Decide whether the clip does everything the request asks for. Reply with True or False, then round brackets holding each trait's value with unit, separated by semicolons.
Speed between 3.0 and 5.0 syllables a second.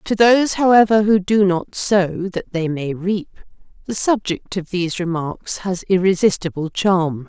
True (4.5 syllables/s)